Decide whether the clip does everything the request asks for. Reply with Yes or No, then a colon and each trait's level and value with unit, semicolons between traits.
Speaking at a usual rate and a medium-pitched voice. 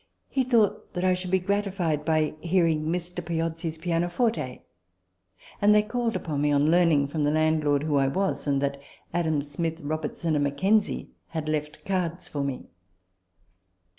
Yes: average, 165 wpm; medium, 160 Hz